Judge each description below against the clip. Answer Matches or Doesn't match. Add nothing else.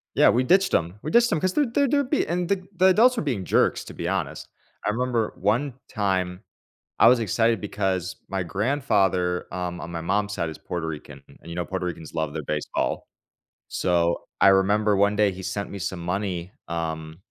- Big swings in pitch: Matches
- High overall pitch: Doesn't match